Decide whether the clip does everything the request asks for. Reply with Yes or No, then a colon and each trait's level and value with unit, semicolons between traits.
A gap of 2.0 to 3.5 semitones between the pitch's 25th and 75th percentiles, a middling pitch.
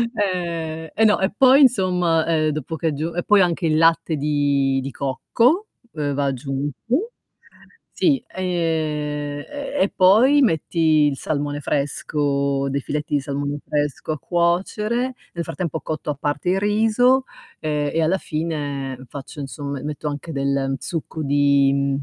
No: average, 4.2 semitones; medium, 155 Hz